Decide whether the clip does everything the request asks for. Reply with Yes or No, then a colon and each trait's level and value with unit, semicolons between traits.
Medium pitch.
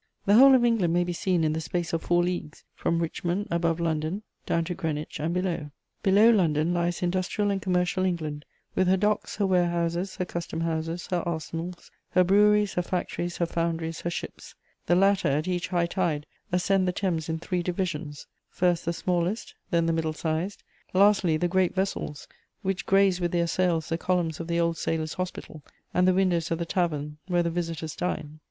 Yes: medium, 175 Hz